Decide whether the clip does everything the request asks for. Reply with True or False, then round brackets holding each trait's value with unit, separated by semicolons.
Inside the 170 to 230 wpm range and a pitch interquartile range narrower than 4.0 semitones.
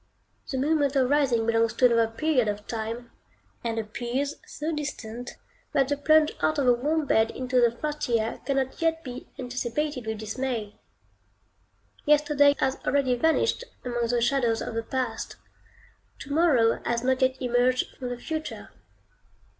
False (155 wpm; 3.6 semitones)